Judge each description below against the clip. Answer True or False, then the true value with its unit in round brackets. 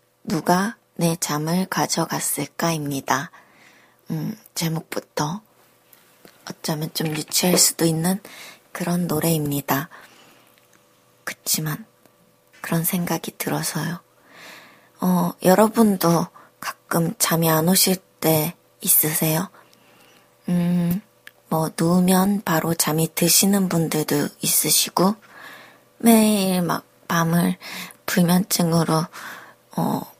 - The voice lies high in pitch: False (170 Hz)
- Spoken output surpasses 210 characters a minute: False (190 characters per minute)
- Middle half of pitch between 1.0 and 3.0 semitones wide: True (2.5 semitones)